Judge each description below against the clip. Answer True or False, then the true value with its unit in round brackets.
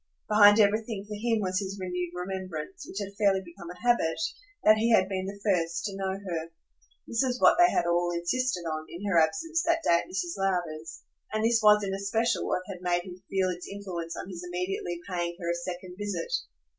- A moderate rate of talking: False (210 wpm)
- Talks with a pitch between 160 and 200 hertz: True (190 Hz)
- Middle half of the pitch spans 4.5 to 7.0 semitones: False (3.2 semitones)